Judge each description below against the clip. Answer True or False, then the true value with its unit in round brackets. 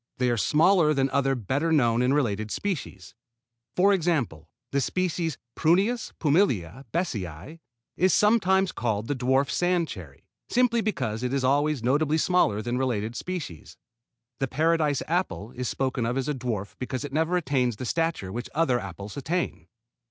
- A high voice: False (135 Hz)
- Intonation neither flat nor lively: False (5.9 semitones)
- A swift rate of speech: False (160 wpm)